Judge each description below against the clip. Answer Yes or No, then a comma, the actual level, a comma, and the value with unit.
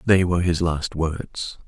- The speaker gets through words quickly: No, average, 180 wpm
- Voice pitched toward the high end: No, very low, 85 Hz